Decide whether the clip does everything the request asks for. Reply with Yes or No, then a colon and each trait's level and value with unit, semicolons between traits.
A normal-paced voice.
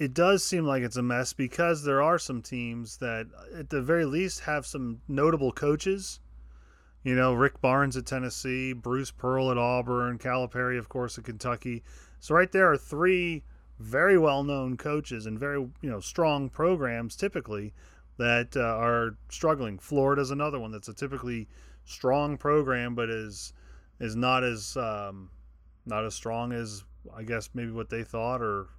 Yes: average, 170 wpm